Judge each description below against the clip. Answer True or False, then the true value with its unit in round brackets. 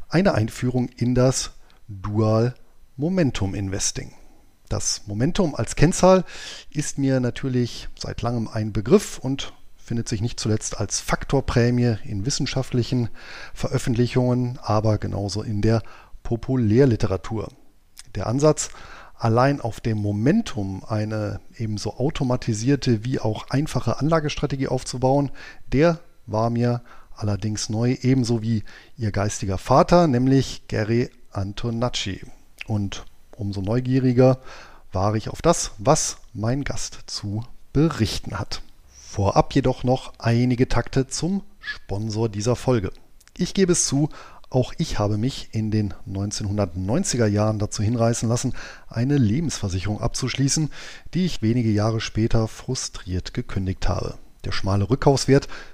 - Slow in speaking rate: True (120 wpm)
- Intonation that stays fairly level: False (3.8 semitones)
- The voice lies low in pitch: True (120 Hz)